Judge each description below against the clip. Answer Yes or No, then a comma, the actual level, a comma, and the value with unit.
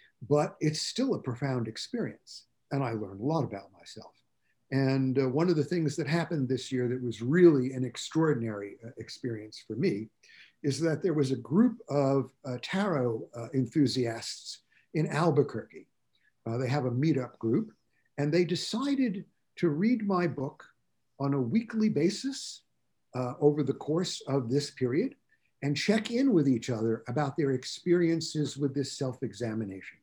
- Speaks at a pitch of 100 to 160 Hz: Yes, medium, 140 Hz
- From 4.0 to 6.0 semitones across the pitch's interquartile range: Yes, average, 4.9 semitones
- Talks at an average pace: Yes, average, 160 wpm